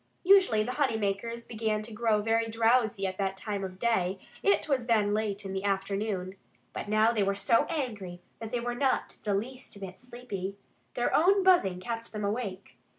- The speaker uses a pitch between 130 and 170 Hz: No, high, 215 Hz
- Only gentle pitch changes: No, average, 3.2 semitones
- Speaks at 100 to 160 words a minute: No, average, 190 wpm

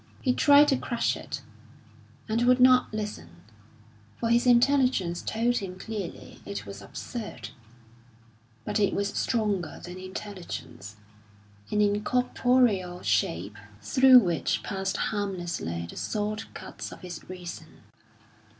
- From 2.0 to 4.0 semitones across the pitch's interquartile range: No, wide, 5.4 semitones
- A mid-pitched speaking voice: No, high, 205 Hz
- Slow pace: Yes, slow, 120 wpm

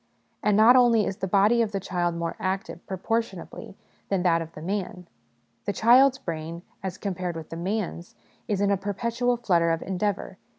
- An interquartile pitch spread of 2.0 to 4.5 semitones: Yes, average, 3.8 semitones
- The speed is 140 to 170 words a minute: No, average, 185 wpm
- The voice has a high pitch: Yes, high, 195 Hz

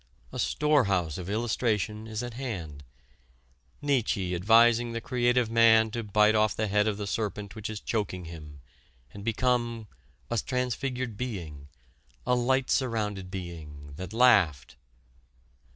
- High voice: No, low, 110 Hz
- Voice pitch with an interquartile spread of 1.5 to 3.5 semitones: No, average, 4.2 semitones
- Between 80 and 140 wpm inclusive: Yes, slow, 135 wpm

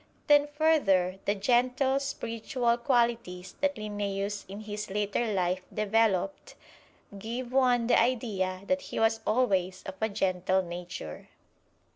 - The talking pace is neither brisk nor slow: No, slow, 125 wpm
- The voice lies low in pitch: No, high, 215 Hz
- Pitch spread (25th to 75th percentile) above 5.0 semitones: No, average, 4.5 semitones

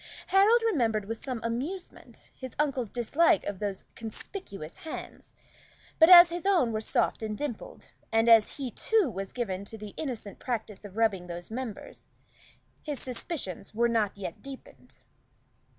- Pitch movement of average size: No, wide, 6.0 semitones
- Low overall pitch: No, high, 235 Hz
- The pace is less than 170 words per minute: Yes, average, 150 wpm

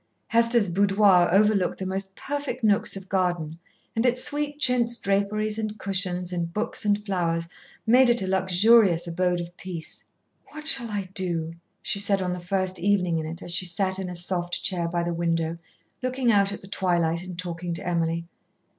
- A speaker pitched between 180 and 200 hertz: Yes, high, 190 Hz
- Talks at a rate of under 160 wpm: No, average, 185 wpm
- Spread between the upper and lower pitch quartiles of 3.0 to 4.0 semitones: Yes, average, 3.4 semitones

